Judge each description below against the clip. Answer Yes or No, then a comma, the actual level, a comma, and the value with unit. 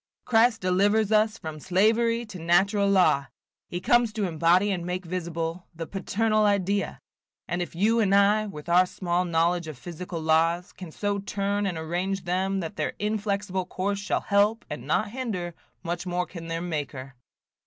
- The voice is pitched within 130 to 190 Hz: Yes, medium, 185 Hz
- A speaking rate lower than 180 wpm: Yes, average, 170 wpm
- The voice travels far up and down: No, average, 3.1 semitones